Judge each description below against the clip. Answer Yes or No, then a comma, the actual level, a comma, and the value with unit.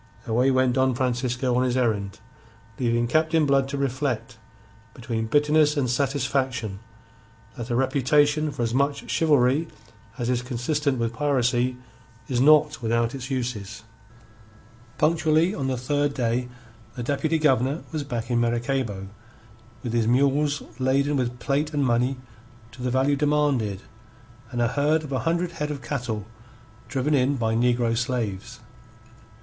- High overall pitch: No, low, 130 Hz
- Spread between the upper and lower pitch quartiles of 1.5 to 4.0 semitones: Yes, average, 3.3 semitones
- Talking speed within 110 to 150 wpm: Yes, average, 145 wpm